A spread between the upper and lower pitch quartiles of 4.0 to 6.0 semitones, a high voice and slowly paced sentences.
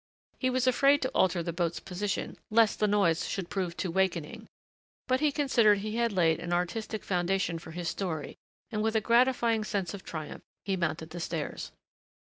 No: average, 4.7 semitones; high, 195 Hz; average, 185 wpm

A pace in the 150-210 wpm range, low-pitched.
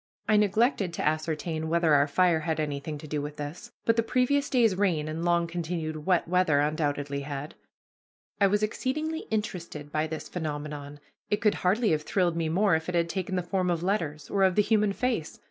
No: average, 200 wpm; medium, 170 Hz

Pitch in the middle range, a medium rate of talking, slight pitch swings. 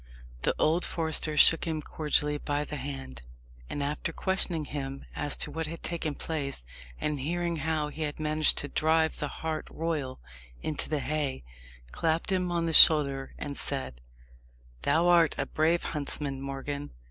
Yes: medium, 150 Hz; average, 160 wpm; narrow, 2.2 semitones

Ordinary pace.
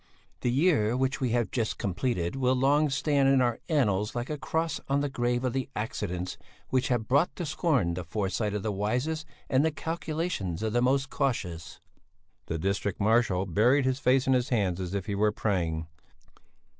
Yes: average, 190 wpm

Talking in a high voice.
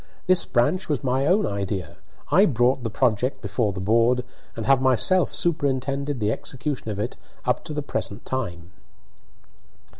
No: low, 125 Hz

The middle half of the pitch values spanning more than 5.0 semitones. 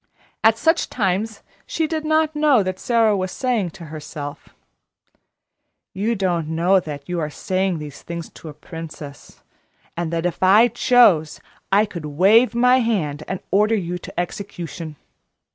Yes: wide, 5.6 semitones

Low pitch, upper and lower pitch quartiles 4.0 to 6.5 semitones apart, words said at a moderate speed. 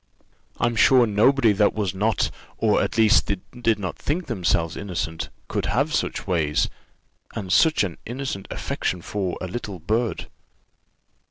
Yes: low, 105 Hz; average, 4.4 semitones; average, 150 wpm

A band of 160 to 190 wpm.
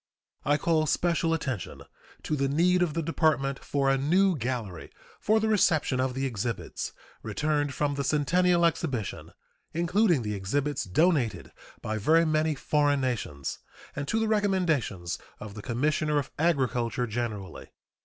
No: average, 145 wpm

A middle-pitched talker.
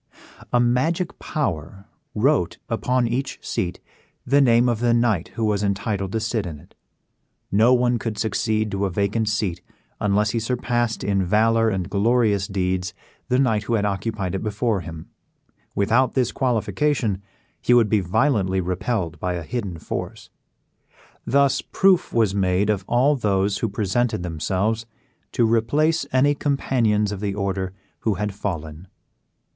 No: low, 110 Hz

